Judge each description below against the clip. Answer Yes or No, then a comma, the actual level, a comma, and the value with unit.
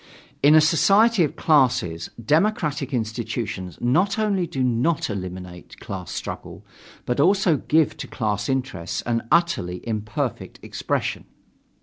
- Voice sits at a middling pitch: No, low, 130 Hz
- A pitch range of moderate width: No, wide, 8.1 semitones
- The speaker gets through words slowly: Yes, slow, 120 wpm